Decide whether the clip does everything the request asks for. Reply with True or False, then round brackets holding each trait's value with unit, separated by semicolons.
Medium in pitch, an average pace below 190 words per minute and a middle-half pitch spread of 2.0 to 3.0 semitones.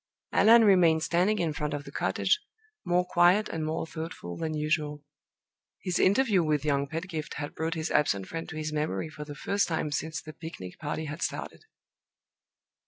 True (160 Hz; 175 wpm; 2.7 semitones)